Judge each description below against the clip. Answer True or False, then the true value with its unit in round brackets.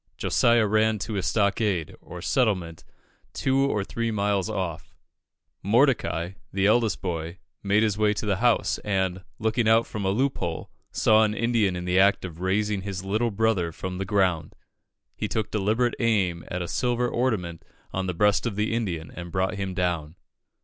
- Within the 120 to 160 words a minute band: False (175 wpm)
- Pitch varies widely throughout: False (3.4 semitones)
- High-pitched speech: False (100 Hz)